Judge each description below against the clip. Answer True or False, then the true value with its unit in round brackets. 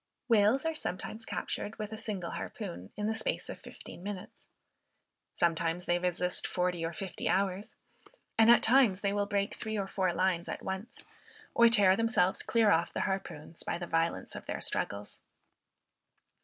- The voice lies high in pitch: True (195 Hz)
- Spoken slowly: False (170 wpm)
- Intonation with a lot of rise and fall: False (3.7 semitones)